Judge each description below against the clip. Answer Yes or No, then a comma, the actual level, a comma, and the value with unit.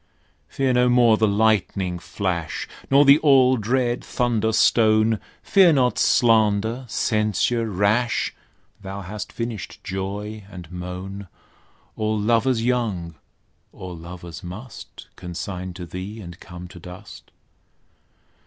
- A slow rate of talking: Yes, slow, 115 wpm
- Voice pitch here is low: Yes, low, 105 Hz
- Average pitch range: Yes, average, 4.4 semitones